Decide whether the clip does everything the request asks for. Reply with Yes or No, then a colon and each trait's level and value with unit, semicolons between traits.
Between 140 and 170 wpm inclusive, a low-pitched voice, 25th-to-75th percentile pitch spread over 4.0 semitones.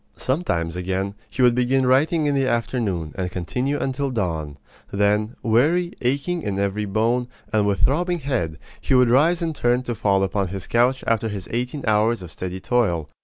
No: average, 180 wpm; low, 115 Hz; average, 5.2 semitones